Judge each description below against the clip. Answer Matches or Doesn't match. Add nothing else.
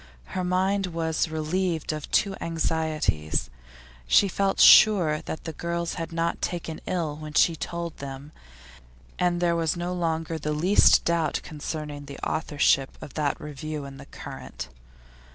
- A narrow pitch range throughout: Matches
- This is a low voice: Doesn't match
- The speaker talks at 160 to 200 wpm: Doesn't match